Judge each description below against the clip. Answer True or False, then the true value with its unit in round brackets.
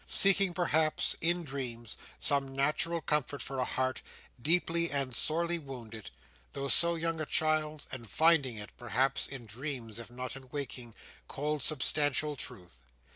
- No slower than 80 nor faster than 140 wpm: True (135 wpm)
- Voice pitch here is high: False (140 Hz)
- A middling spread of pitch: True (3.9 semitones)